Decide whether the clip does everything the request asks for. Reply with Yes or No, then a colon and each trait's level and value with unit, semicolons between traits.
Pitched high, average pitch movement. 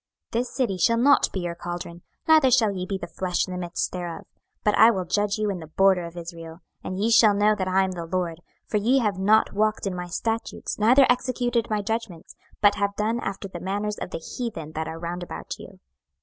Yes: high, 195 Hz; average, 4.0 semitones